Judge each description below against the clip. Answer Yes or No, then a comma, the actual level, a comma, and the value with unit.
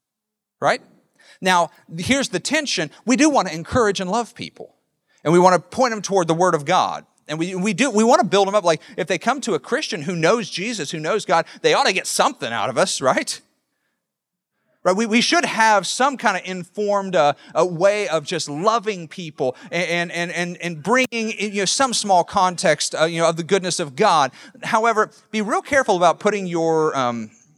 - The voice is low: No, high, 195 Hz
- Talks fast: Yes, fast, 215 wpm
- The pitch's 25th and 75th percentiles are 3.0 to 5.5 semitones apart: Yes, average, 4.6 semitones